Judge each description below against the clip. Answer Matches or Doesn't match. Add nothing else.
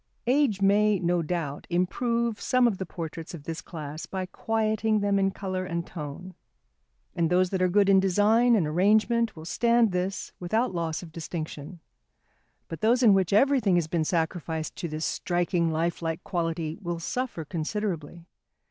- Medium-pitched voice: Matches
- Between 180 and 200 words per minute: Doesn't match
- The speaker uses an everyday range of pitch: Matches